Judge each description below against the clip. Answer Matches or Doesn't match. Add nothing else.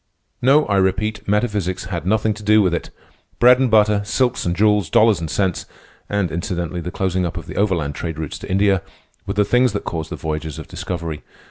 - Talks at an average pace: Doesn't match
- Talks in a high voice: Doesn't match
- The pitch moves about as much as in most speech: Matches